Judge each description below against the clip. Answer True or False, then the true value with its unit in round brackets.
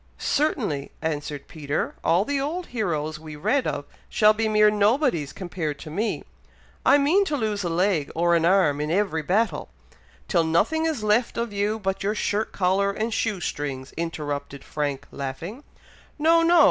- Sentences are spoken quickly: False (170 wpm)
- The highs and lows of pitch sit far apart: True (6.4 semitones)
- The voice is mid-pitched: False (195 Hz)